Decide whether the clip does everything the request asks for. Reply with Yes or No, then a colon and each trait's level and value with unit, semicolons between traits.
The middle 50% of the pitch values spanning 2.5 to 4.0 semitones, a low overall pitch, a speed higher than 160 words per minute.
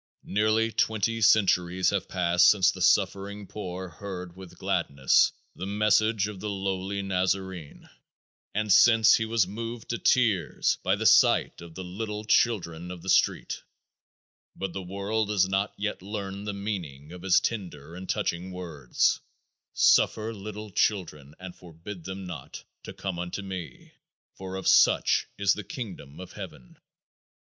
No: average, 2.8 semitones; very low, 95 Hz; average, 150 wpm